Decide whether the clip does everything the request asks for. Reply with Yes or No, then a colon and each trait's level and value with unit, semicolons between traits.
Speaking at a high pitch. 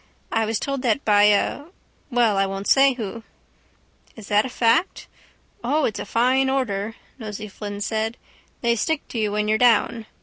Yes: high, 225 Hz